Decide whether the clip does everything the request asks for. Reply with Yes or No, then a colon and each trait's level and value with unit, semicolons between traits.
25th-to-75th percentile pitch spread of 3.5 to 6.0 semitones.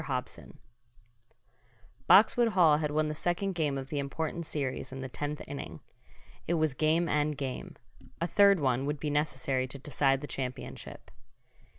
No: average, 2.9 semitones